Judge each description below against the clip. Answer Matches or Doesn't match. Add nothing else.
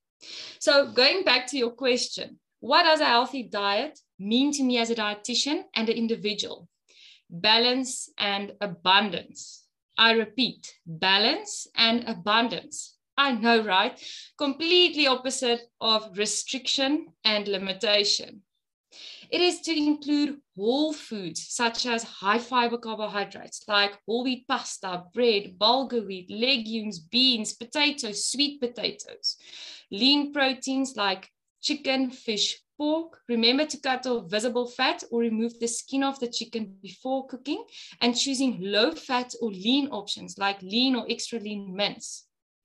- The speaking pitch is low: Doesn't match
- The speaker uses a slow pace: Matches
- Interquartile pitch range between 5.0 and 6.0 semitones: Doesn't match